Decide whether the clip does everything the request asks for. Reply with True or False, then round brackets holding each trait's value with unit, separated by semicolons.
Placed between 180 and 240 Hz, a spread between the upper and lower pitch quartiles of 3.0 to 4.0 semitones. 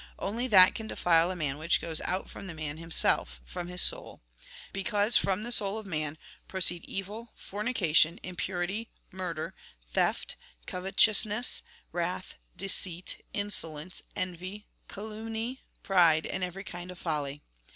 True (185 Hz; 3.7 semitones)